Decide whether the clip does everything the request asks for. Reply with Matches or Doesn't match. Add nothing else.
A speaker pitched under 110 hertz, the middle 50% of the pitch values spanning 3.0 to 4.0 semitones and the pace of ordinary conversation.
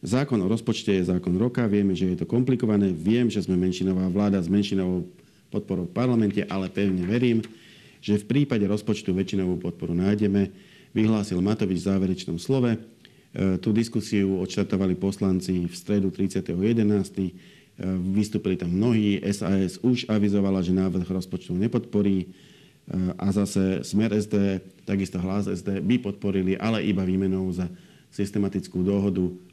Doesn't match